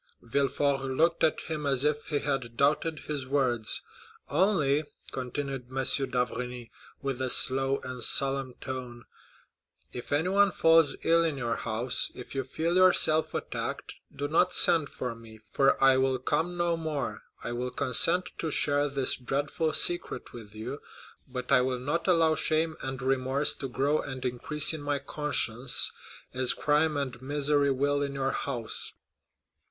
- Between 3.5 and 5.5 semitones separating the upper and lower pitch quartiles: No, average, 3.0 semitones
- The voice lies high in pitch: No, medium, 140 Hz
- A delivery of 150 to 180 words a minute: Yes, average, 155 wpm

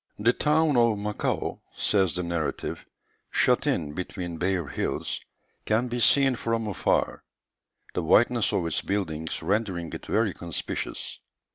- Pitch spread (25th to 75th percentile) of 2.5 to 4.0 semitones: No, average, 4.9 semitones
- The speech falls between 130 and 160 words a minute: Yes, slow, 135 wpm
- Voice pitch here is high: No, low, 100 Hz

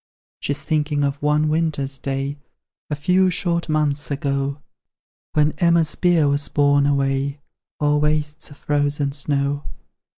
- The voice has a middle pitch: Yes, medium, 145 Hz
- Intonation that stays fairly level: Yes, narrow, 1.5 semitones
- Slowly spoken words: Yes, slow, 130 wpm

